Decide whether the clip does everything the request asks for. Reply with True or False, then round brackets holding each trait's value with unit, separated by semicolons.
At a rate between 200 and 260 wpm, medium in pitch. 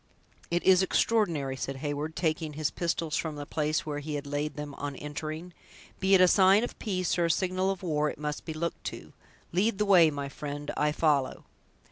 True (205 wpm; 155 Hz)